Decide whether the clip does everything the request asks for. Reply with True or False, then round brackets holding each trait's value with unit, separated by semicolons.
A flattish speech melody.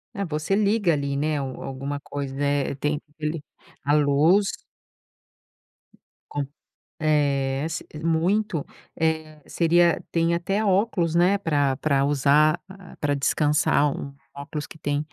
False (3.0 semitones)